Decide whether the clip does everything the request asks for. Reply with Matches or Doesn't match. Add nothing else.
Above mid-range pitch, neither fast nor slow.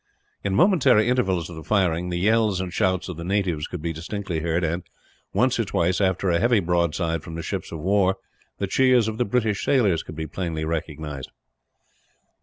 Doesn't match